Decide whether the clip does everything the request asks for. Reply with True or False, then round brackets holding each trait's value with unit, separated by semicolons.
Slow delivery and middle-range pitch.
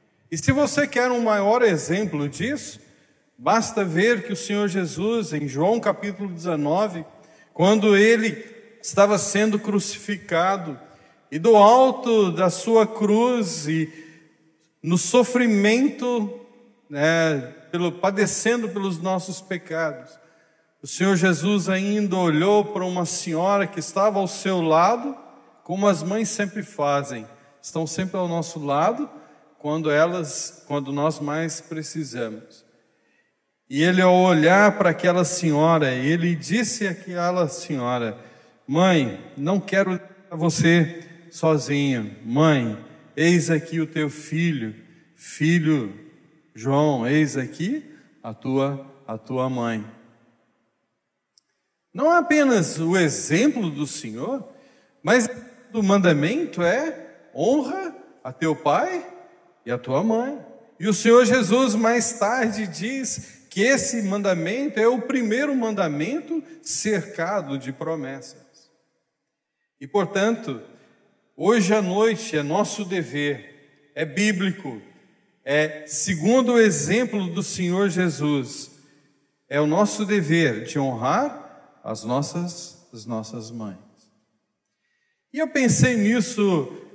True (115 wpm; 180 Hz)